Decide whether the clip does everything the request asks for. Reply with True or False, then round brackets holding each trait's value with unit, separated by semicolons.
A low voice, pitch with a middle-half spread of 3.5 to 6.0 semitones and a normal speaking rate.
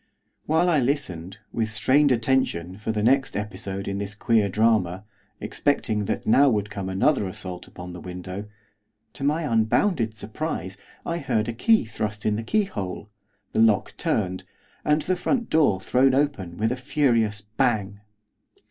True (110 Hz; 5.4 semitones; 155 wpm)